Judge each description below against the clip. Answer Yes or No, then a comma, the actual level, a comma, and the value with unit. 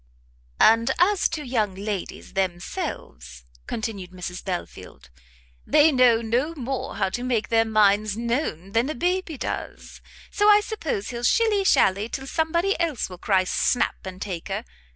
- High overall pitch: Yes, high, 230 Hz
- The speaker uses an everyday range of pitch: No, wide, 7.9 semitones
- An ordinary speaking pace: Yes, average, 150 wpm